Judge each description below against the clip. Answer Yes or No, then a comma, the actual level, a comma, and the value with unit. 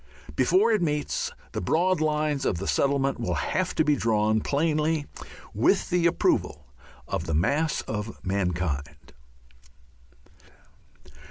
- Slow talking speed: Yes, slow, 115 wpm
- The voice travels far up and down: Yes, wide, 8.1 semitones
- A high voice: No, medium, 140 Hz